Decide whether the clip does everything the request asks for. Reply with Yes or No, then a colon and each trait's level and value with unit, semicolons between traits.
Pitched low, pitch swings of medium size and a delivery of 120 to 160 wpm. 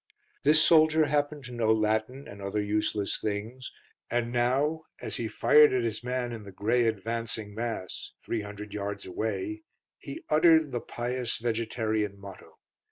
Yes: low, 115 Hz; average, 3.4 semitones; average, 150 wpm